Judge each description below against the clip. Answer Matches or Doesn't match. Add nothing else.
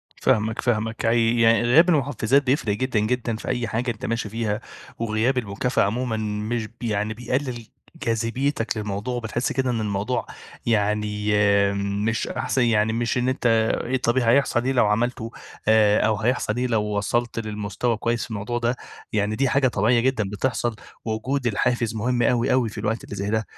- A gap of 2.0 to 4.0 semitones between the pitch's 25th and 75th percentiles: Matches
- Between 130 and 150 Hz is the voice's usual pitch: Doesn't match